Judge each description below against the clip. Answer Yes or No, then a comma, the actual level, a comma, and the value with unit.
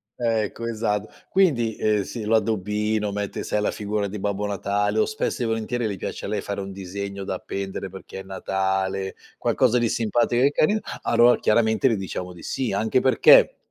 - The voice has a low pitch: Yes, low, 105 Hz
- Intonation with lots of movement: No, average, 2.7 semitones